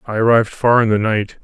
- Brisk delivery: Yes, fast, 250 wpm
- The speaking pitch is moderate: No, low, 110 Hz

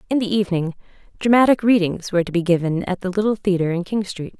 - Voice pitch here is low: No, high, 190 Hz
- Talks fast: Yes, fast, 220 wpm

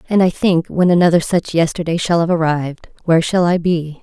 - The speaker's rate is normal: No, fast, 210 wpm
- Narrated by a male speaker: No, female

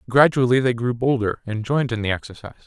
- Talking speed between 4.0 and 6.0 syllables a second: No, 7.0 syllables/s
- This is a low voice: Yes, low, 120 Hz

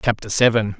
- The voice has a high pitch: No, low, 110 Hz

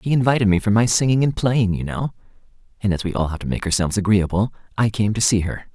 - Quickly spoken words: Yes, fast, 250 wpm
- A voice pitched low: Yes, low, 105 Hz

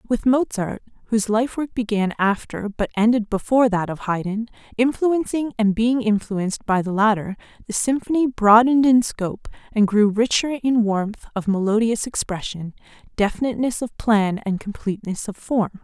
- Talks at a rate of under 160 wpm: Yes, average, 150 wpm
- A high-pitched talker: Yes, high, 220 Hz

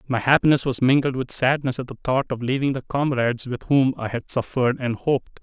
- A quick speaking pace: Yes, fast, 220 wpm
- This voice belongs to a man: Yes, male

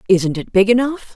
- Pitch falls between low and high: No, high, 210 Hz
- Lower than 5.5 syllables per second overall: Yes, 5.2 syllables/s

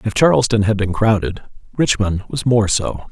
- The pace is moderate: Yes, average, 175 wpm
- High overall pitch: No, low, 110 Hz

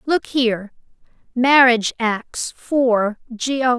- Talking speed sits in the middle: No, slow, 95 wpm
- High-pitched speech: Yes, high, 245 Hz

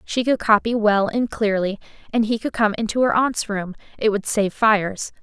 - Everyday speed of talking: Yes, average, 195 wpm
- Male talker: No, female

